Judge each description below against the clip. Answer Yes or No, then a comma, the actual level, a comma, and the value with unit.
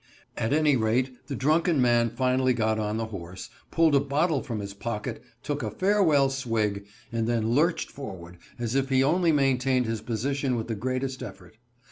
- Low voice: Yes, low, 125 Hz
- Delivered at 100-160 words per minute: No, average, 180 wpm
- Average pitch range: Yes, average, 3.9 semitones